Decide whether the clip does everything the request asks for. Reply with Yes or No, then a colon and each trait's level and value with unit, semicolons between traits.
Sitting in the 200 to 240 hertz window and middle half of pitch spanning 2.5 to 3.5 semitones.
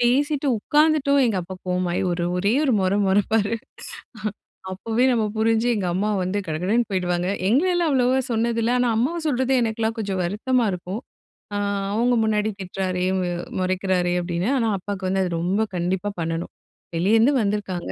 No: high, 210 Hz; average, 4.6 semitones